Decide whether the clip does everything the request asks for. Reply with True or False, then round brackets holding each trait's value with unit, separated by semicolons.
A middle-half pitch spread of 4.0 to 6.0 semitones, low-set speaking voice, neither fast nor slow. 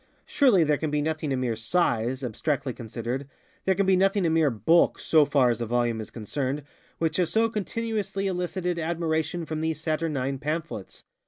False (5.4 semitones; 155 Hz; 175 wpm)